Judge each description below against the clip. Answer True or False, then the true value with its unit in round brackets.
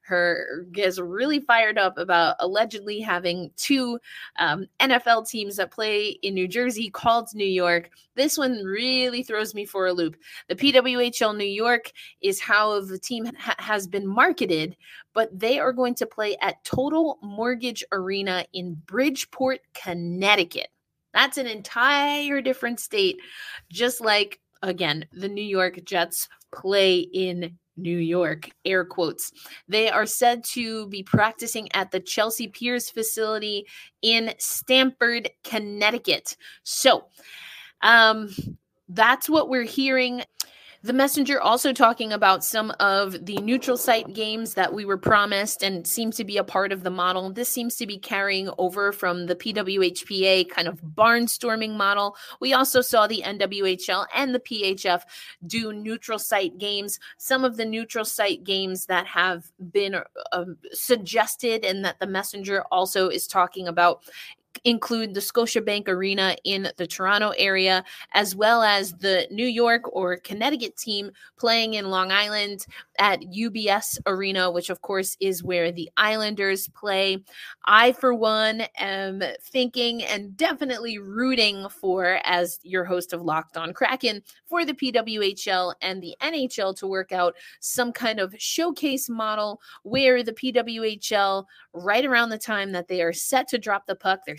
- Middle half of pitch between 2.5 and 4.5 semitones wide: True (4.0 semitones)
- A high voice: True (205 Hz)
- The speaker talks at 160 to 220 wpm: False (150 wpm)